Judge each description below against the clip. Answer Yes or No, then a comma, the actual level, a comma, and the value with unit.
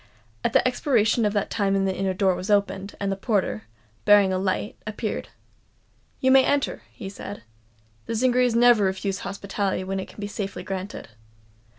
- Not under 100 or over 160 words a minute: No, average, 175 wpm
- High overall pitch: Yes, high, 200 Hz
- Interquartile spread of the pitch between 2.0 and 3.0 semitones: Yes, narrow, 2.6 semitones